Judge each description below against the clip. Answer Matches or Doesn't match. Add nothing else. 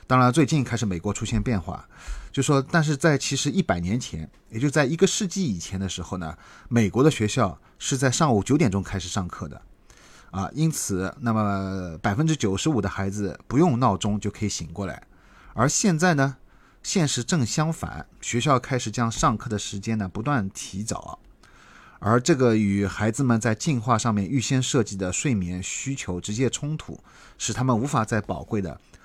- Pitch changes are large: Matches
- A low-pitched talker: Matches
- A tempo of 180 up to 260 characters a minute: Doesn't match